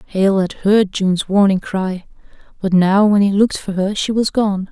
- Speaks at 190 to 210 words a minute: Yes, fast, 205 wpm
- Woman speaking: Yes, female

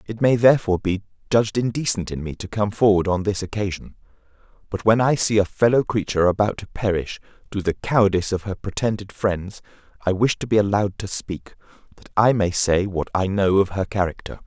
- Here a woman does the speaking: No, male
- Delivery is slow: No, average, 200 wpm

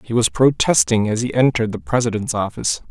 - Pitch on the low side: Yes, low, 115 Hz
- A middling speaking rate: Yes, average, 185 wpm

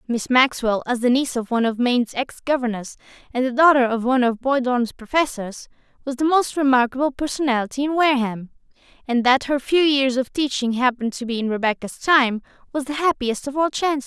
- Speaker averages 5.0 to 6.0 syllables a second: Yes, 5.8 syllables/s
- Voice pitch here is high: Yes, very high, 255 Hz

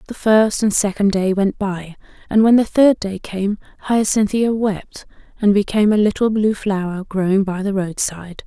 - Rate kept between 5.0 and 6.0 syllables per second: No, 4.8 syllables/s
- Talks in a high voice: Yes, high, 200 Hz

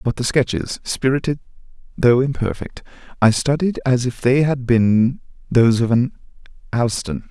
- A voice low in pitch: Yes, low, 125 Hz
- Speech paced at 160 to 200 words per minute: No, average, 140 wpm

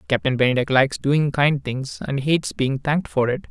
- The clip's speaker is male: Yes, male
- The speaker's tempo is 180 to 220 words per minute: Yes, fast, 205 wpm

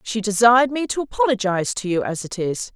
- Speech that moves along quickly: Yes, fast, 220 wpm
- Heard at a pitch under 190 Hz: No, high, 220 Hz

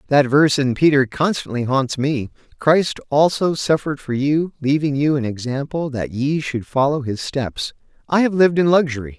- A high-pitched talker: No, medium, 140 Hz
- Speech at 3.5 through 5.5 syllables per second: Yes, 5.0 syllables/s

